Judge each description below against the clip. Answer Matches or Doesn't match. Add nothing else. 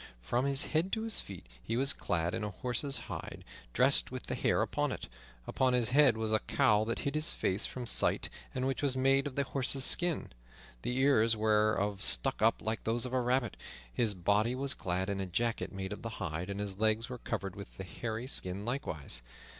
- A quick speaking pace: Matches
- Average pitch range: Matches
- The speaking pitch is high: Doesn't match